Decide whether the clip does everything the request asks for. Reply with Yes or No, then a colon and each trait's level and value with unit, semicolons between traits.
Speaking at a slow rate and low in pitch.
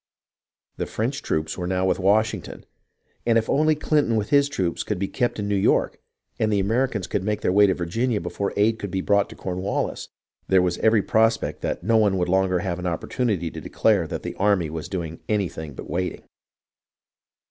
No: average, 200 wpm; low, 100 Hz